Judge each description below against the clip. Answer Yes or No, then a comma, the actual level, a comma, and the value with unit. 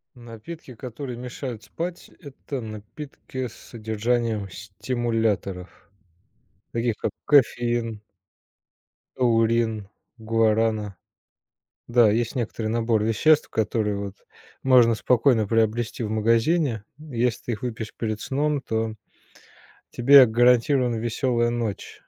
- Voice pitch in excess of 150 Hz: No, low, 115 Hz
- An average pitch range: No, narrow, 2.2 semitones